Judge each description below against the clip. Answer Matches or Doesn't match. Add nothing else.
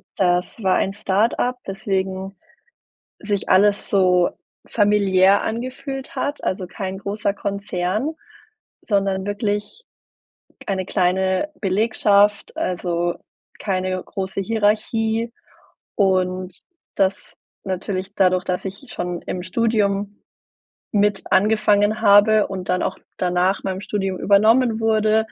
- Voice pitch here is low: Doesn't match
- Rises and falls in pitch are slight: Matches